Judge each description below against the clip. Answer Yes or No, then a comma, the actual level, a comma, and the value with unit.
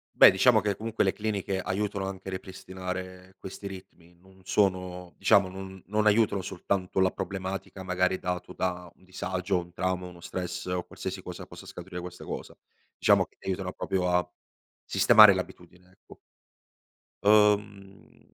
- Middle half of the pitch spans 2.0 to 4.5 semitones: No, narrow, 1.3 semitones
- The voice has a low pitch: Yes, very low, 95 Hz